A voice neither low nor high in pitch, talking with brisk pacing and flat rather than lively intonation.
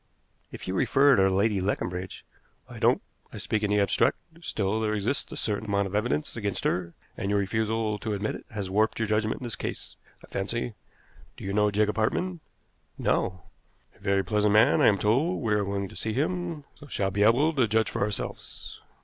No: low, 105 Hz; fast, 210 wpm; narrow, 2.2 semitones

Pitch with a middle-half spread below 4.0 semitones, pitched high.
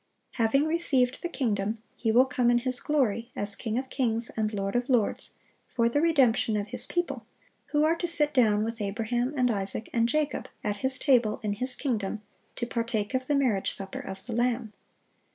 Yes: average, 3.4 semitones; high, 240 Hz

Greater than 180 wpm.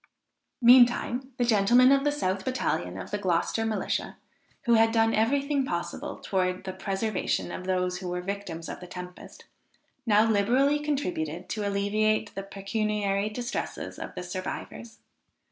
No: average, 155 wpm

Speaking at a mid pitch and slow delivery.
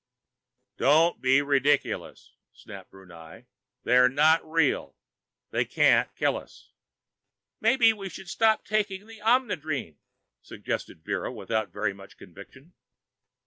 Yes: medium, 145 Hz; slow, 110 wpm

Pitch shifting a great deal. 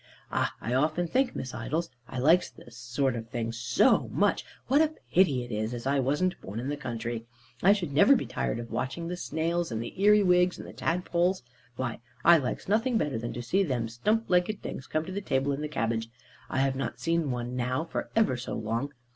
Yes: wide, 6.7 semitones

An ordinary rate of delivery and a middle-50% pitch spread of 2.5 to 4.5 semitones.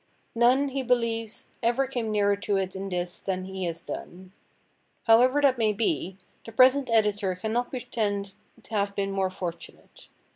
Yes: average, 160 wpm; average, 4.0 semitones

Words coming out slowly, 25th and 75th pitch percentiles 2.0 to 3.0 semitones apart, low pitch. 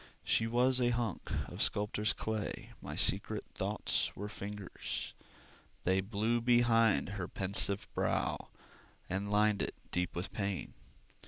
Yes: slow, 130 wpm; narrow, 2.6 semitones; low, 105 Hz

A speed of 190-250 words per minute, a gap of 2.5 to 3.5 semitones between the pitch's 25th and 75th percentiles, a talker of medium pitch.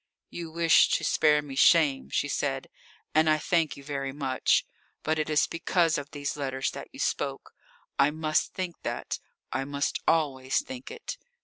No: average, 175 wpm; average, 2.9 semitones; medium, 150 Hz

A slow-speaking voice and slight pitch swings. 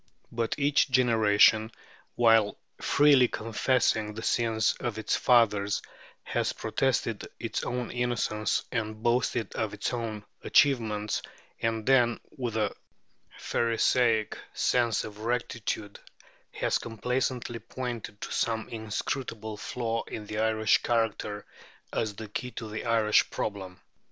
Yes: slow, 120 wpm; narrow, 2.1 semitones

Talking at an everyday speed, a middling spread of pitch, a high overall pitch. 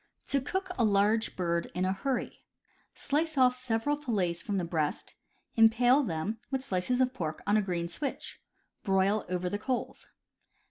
No: average, 170 wpm; wide, 5.9 semitones; high, 215 Hz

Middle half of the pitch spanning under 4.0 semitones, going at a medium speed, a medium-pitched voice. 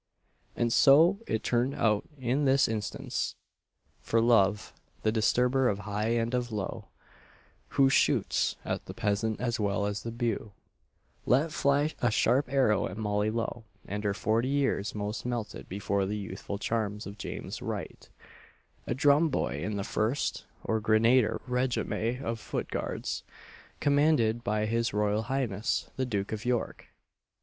No: average, 3.2 semitones; average, 150 wpm; low, 115 Hz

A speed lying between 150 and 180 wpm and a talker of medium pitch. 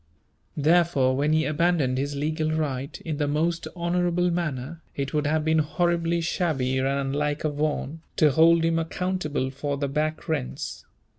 Yes: average, 160 wpm; medium, 155 Hz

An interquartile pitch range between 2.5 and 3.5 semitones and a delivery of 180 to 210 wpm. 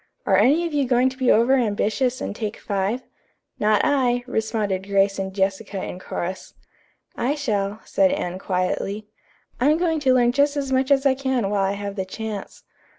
No: average, 5.0 semitones; average, 185 wpm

